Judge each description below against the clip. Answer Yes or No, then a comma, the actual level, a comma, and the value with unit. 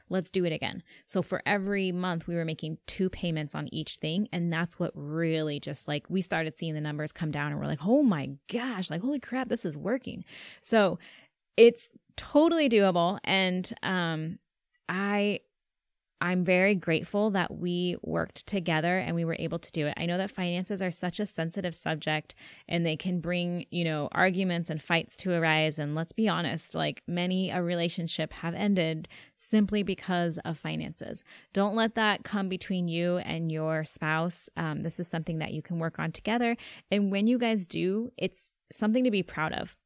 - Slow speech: No, average, 190 wpm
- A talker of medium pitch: Yes, medium, 175 Hz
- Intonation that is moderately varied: Yes, average, 3.5 semitones